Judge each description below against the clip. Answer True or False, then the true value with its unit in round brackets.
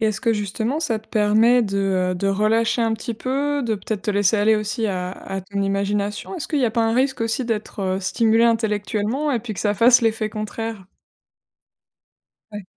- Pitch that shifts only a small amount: True (2.2 semitones)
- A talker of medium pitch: False (220 Hz)